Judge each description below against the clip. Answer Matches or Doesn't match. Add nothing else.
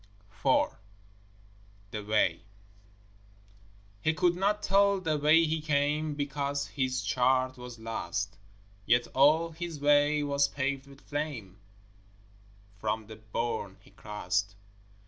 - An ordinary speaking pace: Doesn't match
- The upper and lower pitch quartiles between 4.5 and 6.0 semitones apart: Matches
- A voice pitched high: Doesn't match